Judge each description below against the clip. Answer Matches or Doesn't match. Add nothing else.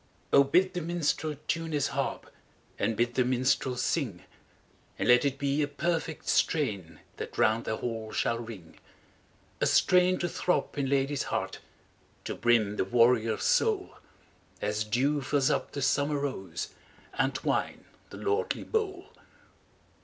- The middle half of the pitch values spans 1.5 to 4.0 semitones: Doesn't match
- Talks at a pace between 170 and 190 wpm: Doesn't match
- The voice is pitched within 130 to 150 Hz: Matches